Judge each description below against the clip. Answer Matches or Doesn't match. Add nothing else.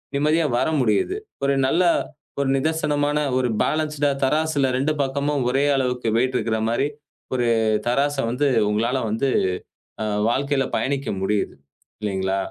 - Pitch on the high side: Doesn't match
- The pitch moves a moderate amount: Matches